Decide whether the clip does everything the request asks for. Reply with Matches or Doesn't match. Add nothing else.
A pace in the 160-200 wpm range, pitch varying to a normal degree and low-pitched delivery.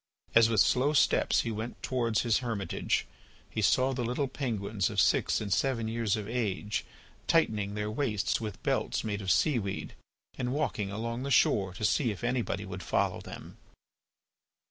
Matches